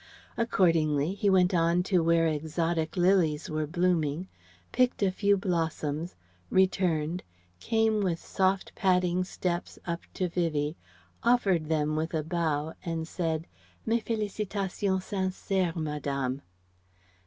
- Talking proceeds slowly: Yes, slow, 115 wpm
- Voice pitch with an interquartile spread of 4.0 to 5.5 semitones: No, average, 3.2 semitones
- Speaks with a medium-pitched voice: Yes, medium, 175 Hz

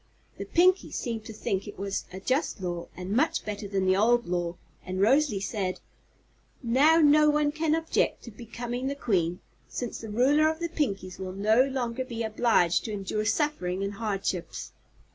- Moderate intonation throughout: No, wide, 6.1 semitones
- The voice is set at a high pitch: Yes, high, 220 Hz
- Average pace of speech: Yes, average, 180 wpm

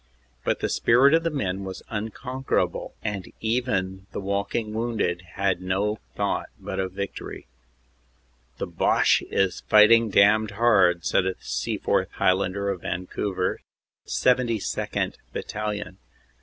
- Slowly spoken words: Yes, slow, 125 wpm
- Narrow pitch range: No, average, 3.1 semitones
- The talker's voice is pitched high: No, low, 100 Hz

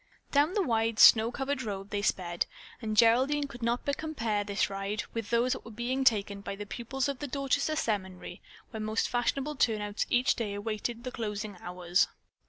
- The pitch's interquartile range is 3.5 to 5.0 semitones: Yes, average, 4.2 semitones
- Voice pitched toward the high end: Yes, high, 225 Hz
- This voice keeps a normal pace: Yes, average, 190 wpm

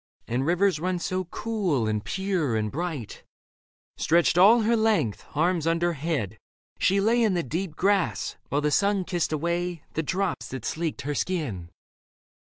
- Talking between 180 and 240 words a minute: No, average, 160 wpm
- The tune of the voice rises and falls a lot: No, average, 4.7 semitones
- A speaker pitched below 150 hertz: No, medium, 170 Hz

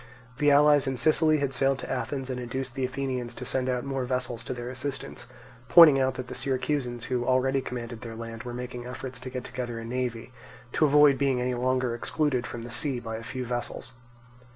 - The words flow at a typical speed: No, fast, 210 wpm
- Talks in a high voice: No, low, 125 Hz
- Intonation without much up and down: Yes, narrow, 1.9 semitones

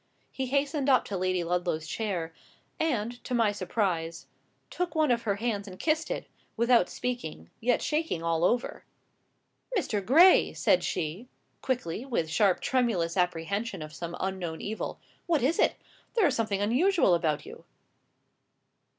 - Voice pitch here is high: Yes, high, 210 Hz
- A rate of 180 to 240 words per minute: No, average, 150 wpm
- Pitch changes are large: Yes, wide, 6.5 semitones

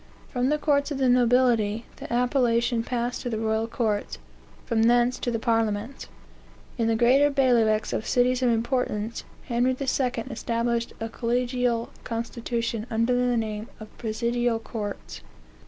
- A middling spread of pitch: No, narrow, 1.7 semitones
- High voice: Yes, high, 235 Hz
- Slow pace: No, average, 145 wpm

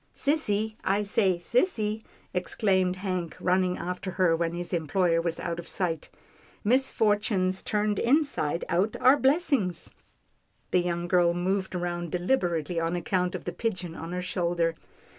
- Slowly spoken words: No, average, 150 wpm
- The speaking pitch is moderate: Yes, medium, 180 Hz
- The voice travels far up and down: No, average, 3.2 semitones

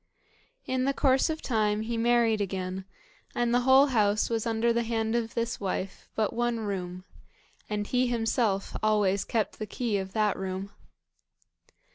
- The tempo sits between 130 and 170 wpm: Yes, average, 160 wpm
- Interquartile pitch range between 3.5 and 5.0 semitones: No, average, 2.9 semitones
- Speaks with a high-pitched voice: Yes, high, 225 Hz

